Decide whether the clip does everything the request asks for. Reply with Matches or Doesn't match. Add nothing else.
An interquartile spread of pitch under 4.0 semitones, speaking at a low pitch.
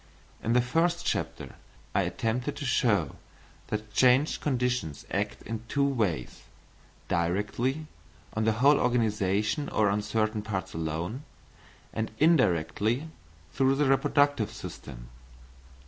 Doesn't match